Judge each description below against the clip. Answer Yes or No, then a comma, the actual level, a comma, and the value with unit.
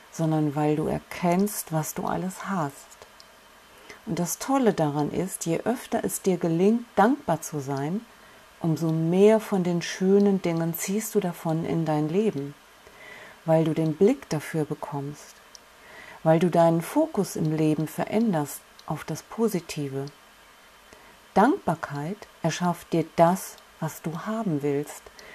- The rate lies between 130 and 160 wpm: Yes, slow, 135 wpm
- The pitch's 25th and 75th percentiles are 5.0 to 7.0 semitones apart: No, average, 4.4 semitones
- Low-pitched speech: No, medium, 170 Hz